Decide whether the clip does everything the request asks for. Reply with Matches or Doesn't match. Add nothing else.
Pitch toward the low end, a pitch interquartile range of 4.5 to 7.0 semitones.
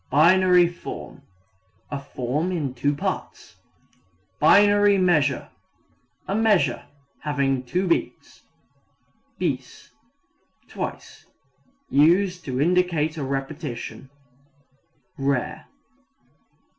Doesn't match